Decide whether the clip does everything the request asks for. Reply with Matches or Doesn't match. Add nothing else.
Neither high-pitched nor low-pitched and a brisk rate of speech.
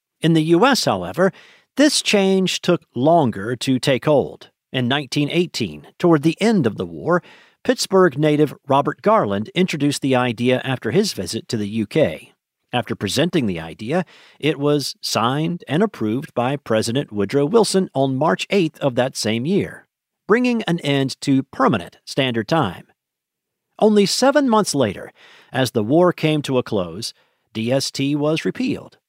Doesn't match